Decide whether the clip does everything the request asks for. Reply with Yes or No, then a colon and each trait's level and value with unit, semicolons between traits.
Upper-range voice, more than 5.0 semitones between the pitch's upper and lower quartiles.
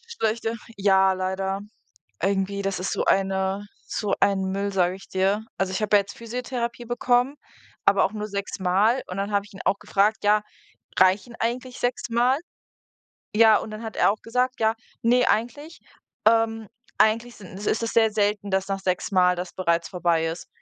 No: high, 205 Hz; average, 3.0 semitones